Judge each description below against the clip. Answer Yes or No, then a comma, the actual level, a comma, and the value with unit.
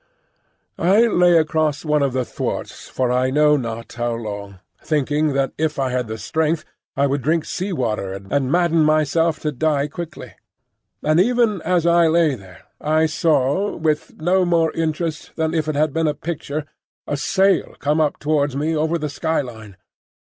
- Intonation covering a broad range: No, average, 3.1 semitones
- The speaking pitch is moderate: Yes, medium, 155 Hz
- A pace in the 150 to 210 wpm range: Yes, average, 175 wpm